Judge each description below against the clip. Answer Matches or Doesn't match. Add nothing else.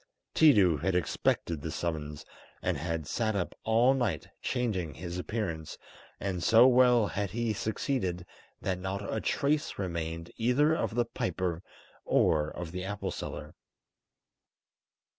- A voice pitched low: Matches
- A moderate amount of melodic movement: Doesn't match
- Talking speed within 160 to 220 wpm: Doesn't match